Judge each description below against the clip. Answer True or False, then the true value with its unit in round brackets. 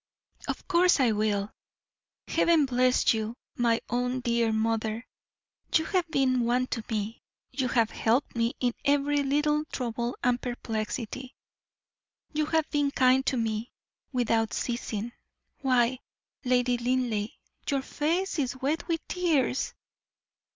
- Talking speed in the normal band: False (130 wpm)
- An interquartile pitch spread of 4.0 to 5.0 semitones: False (3.5 semitones)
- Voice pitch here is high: True (250 Hz)